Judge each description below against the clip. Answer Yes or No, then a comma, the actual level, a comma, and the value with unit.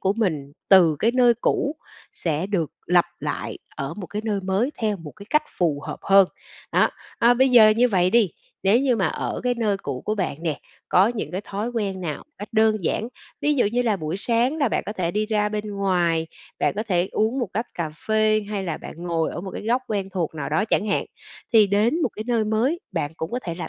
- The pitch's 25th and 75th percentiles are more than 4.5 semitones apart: No, average, 4.2 semitones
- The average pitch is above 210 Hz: No, high, 205 Hz